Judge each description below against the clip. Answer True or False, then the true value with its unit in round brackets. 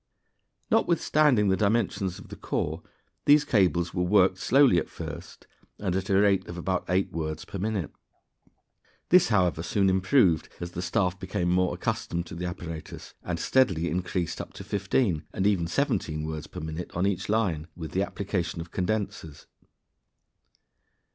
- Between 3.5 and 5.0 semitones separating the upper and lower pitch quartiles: False (2.9 semitones)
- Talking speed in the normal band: True (160 wpm)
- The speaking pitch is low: True (95 Hz)